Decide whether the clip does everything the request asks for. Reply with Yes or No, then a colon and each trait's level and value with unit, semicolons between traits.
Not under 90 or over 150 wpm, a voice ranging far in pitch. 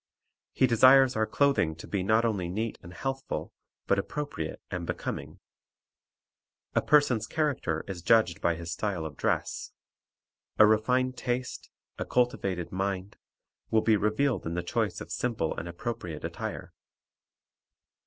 Yes: average, 140 wpm; wide, 6.1 semitones